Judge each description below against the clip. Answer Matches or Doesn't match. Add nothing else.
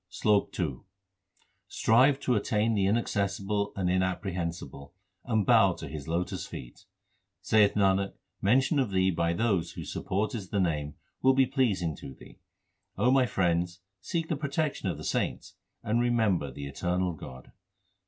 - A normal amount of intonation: Matches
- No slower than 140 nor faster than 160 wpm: Matches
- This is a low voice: Matches